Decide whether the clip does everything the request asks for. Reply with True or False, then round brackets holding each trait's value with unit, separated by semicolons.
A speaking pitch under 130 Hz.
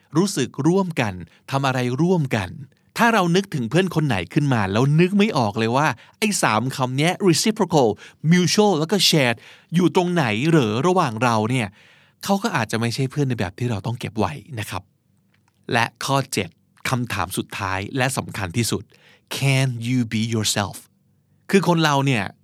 False (135 Hz)